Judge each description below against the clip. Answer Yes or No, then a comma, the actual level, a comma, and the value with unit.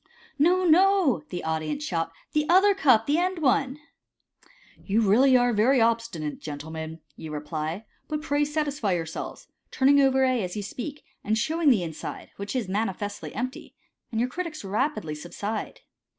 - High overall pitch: Yes, high, 235 Hz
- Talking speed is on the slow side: No, average, 170 wpm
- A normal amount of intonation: No, wide, 8.3 semitones